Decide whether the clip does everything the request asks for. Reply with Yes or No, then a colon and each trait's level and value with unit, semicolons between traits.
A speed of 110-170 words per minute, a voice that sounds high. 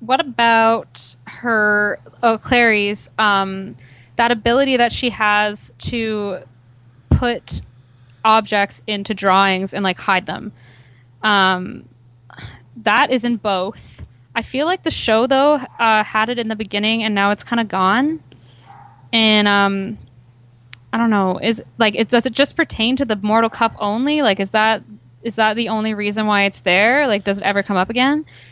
Yes: average, 160 wpm; high, 210 Hz